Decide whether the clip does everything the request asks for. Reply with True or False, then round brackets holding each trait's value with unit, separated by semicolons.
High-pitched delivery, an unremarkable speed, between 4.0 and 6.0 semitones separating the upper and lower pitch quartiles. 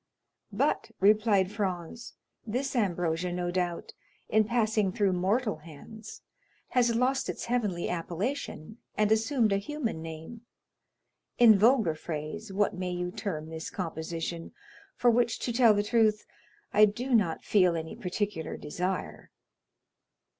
False (205 Hz; 130 wpm; 4.3 semitones)